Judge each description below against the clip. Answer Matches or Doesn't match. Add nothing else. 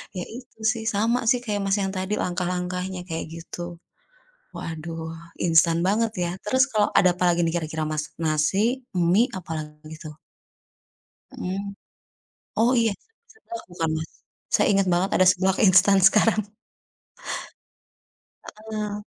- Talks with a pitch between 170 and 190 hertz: Matches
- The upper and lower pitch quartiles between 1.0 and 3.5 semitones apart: Doesn't match